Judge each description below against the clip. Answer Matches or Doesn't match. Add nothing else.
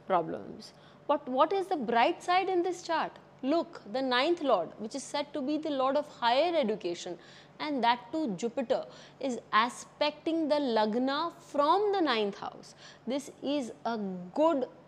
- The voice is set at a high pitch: Matches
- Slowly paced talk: Doesn't match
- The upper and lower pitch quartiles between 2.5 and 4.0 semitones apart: Doesn't match